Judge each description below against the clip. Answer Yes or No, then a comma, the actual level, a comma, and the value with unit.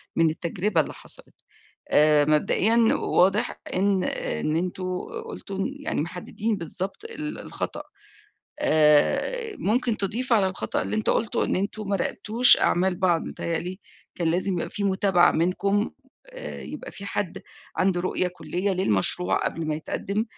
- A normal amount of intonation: Yes, average, 3.9 semitones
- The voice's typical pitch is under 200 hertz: Yes, high, 190 Hz